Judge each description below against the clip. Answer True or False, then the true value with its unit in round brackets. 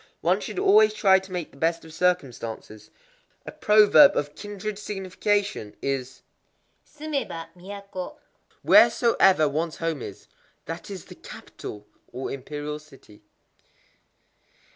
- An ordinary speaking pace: False (120 wpm)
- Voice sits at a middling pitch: True (180 Hz)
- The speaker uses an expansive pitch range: True (5.8 semitones)